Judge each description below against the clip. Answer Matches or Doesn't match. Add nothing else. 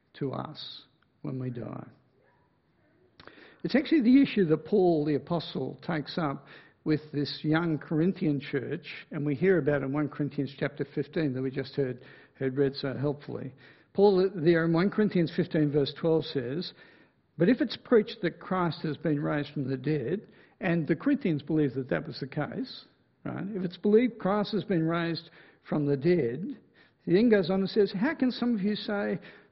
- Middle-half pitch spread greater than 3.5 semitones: Matches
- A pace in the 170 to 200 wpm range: Matches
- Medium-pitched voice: Matches